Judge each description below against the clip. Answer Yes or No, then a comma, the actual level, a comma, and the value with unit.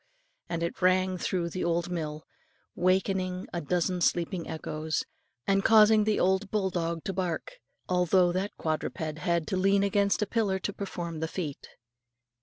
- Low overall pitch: No, medium, 180 Hz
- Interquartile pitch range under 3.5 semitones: Yes, narrow, 2.5 semitones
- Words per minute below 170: Yes, average, 155 wpm